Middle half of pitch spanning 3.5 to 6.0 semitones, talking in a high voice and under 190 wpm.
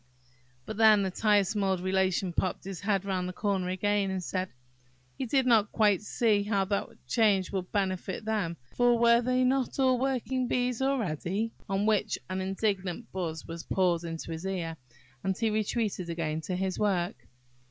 No: average, 3.1 semitones; high, 195 Hz; average, 170 wpm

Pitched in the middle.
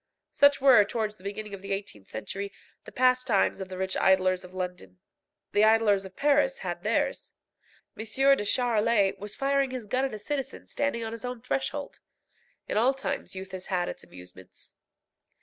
No: high, 210 Hz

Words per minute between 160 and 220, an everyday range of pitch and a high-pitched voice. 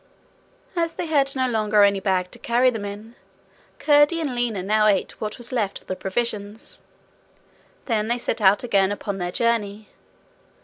Yes: average, 170 wpm; average, 3.3 semitones; high, 215 Hz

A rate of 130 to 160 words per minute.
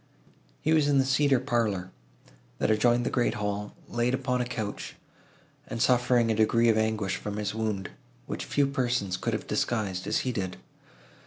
No: average, 175 wpm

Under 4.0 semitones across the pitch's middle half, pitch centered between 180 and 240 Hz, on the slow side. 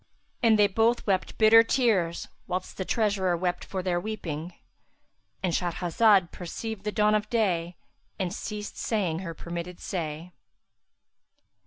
Yes: average, 3.6 semitones; high, 190 Hz; slow, 130 wpm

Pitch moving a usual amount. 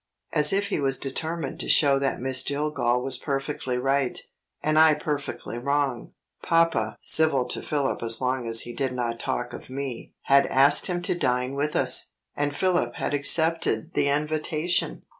Yes: average, 3.3 semitones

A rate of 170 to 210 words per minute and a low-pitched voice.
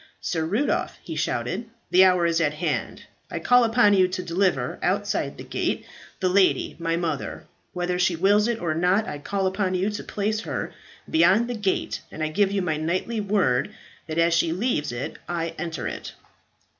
No: average, 190 wpm; medium, 180 Hz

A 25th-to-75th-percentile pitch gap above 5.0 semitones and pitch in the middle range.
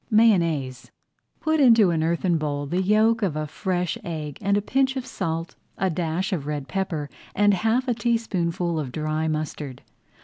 Yes: wide, 5.6 semitones; medium, 175 Hz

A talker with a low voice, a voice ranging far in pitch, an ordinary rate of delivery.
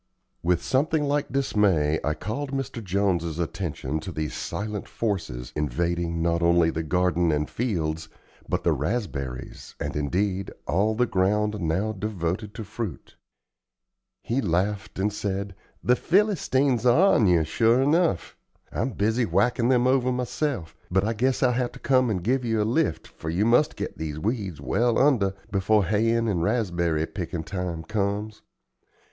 Yes: low, 100 Hz; wide, 6.0 semitones; average, 155 wpm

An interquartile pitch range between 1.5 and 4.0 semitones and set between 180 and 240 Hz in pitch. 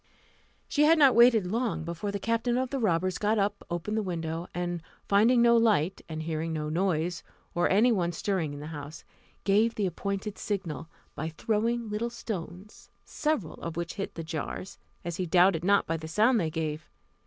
No: average, 5.0 semitones; high, 190 Hz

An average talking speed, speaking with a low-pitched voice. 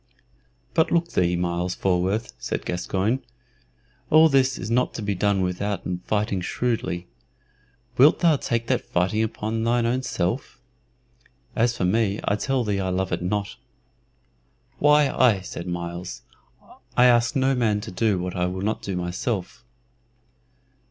Yes: average, 150 wpm; low, 105 Hz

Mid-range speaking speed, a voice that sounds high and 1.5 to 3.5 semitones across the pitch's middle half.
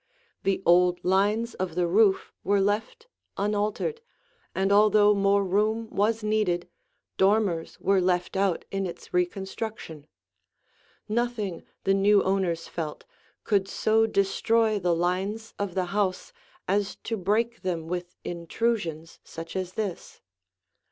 No: slow, 125 wpm; high, 195 Hz; average, 3.0 semitones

